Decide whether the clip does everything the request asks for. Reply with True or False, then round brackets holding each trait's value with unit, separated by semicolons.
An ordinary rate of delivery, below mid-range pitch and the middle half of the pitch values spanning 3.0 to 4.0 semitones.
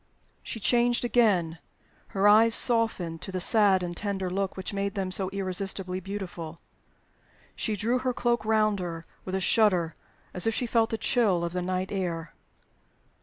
False (170 wpm; 195 Hz; 3.4 semitones)